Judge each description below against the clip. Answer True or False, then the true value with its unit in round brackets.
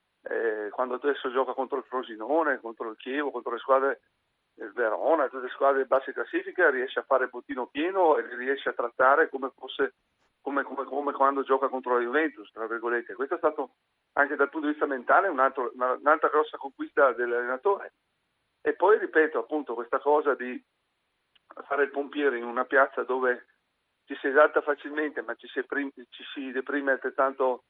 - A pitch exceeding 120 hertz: True (140 Hz)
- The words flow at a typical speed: False (175 wpm)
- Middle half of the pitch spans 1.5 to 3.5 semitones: True (3.2 semitones)